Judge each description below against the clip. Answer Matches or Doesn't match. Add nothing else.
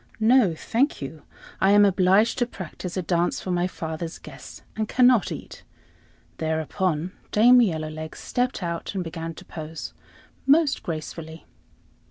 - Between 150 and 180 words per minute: Doesn't match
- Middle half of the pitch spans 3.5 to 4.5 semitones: Doesn't match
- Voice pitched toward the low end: Doesn't match